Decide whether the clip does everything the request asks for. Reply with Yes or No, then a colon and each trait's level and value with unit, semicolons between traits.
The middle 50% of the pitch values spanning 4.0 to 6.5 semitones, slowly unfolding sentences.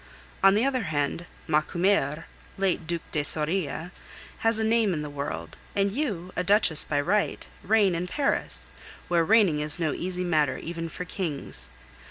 No: average, 4.6 semitones; average, 165 wpm